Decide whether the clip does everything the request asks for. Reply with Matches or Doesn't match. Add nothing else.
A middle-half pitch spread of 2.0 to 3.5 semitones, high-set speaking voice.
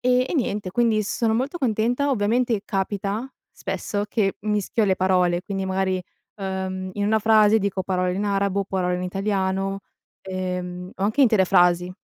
Matches